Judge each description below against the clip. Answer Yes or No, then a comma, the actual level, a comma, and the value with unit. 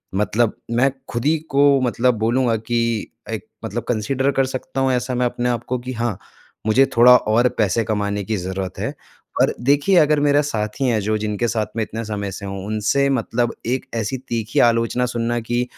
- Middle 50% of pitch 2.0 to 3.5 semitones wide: Yes, average, 3.1 semitones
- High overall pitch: No, low, 120 Hz